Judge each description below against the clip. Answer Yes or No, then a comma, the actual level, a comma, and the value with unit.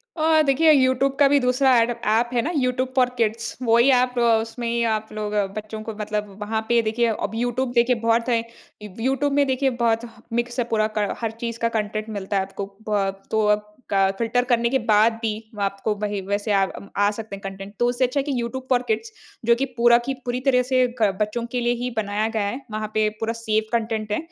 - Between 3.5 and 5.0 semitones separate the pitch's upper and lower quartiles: No, average, 2.8 semitones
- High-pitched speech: Yes, high, 230 Hz